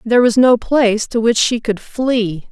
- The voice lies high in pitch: Yes, high, 230 Hz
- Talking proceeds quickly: Yes, fast, 215 wpm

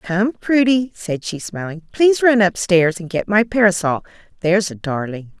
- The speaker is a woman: Yes, female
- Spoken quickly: No, average, 165 wpm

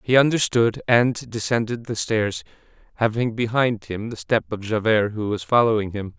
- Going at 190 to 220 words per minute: No, average, 165 wpm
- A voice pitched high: No, low, 115 Hz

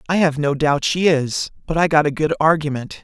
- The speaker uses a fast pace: Yes, fast, 235 wpm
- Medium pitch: Yes, medium, 150 Hz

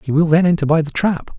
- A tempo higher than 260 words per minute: Yes, fast, 305 wpm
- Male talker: Yes, male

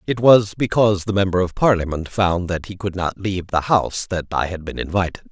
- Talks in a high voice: No, very low, 95 Hz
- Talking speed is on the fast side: Yes, fast, 225 wpm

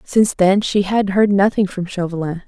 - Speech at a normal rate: Yes, average, 195 wpm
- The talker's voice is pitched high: Yes, high, 195 Hz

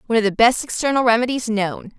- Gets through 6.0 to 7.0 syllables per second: Yes, 6.3 syllables/s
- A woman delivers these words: Yes, female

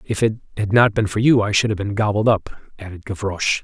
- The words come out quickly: Yes, fast, 250 wpm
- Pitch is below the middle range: Yes, low, 105 Hz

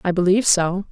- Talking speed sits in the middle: Yes, average, 195 wpm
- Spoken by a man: No, female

